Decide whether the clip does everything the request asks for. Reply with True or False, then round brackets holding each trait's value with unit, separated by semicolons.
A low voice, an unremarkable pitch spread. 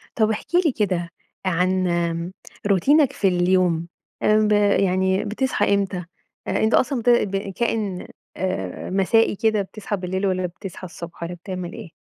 False (190 Hz; 3.1 semitones)